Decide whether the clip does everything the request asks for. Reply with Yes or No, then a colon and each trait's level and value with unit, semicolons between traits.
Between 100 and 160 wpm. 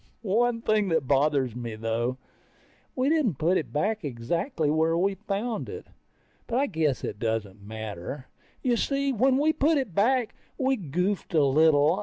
No: average, 170 wpm